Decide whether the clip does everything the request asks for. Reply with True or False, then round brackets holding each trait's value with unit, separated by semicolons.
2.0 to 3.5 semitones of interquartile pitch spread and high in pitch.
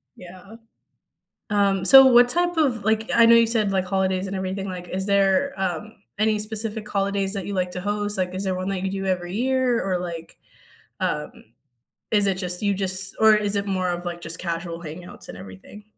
True (2.6 semitones; 195 Hz)